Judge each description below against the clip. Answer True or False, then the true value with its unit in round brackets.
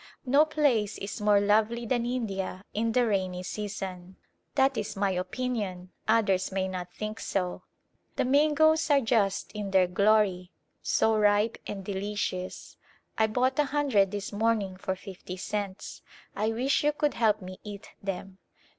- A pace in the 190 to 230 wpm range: False (155 wpm)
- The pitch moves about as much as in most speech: True (3.7 semitones)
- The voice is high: True (210 Hz)